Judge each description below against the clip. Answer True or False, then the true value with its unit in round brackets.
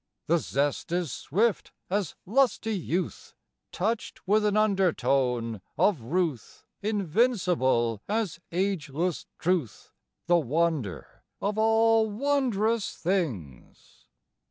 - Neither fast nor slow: False (95 wpm)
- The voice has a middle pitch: True (180 Hz)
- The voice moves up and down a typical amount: False (6.6 semitones)